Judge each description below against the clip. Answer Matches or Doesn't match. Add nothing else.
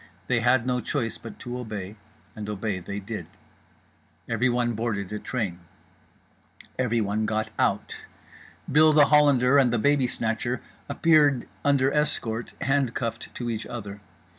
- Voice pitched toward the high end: Doesn't match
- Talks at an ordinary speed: Doesn't match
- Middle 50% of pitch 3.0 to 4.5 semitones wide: Matches